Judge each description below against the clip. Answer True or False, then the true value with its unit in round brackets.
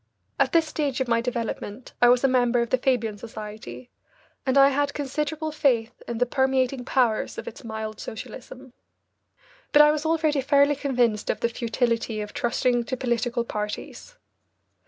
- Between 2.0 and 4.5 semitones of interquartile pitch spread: True (3.2 semitones)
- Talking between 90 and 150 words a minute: False (165 wpm)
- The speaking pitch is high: True (250 Hz)